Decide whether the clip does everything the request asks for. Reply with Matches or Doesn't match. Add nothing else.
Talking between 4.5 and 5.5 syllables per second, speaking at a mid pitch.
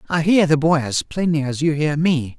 Matches